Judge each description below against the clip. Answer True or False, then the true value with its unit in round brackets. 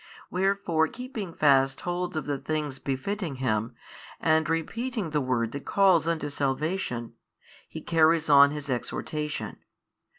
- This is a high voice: False (155 Hz)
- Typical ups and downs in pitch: True (4.3 semitones)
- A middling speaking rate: False (130 wpm)